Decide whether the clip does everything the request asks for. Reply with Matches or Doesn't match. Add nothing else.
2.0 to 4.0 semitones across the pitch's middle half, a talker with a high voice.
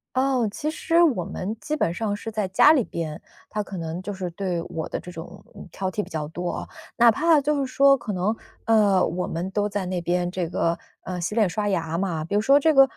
Doesn't match